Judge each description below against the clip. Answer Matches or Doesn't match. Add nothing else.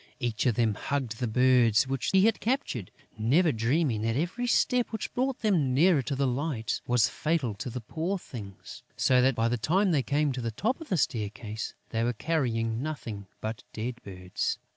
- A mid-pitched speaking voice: Doesn't match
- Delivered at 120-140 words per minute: Doesn't match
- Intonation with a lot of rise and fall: Matches